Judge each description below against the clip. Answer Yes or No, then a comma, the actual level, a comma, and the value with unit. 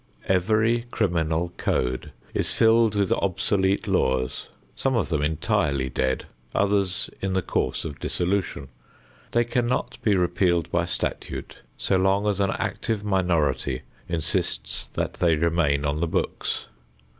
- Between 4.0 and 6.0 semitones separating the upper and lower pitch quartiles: Yes, average, 4.4 semitones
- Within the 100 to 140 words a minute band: Yes, slow, 135 wpm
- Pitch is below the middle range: Yes, very low, 90 Hz